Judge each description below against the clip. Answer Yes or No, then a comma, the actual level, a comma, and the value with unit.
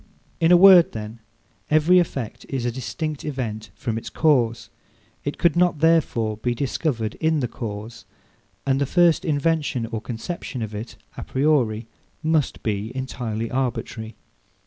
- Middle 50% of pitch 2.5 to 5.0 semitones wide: No, wide, 5.6 semitones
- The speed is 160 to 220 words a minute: No, average, 145 wpm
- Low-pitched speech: Yes, low, 130 Hz